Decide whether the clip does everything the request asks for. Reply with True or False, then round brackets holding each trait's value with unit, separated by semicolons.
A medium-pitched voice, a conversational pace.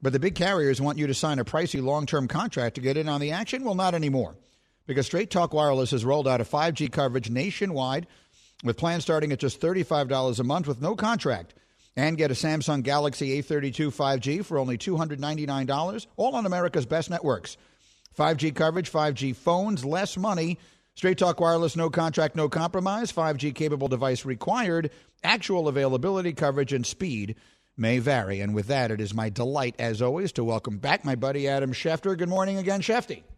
True (150 Hz; 185 wpm)